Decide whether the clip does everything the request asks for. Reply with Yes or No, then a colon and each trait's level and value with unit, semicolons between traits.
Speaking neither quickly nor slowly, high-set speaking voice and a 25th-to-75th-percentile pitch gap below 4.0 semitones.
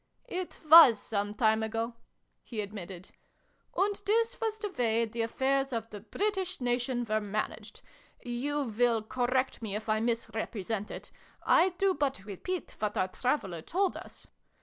No: average, 155 wpm; high, 240 Hz; wide, 5.5 semitones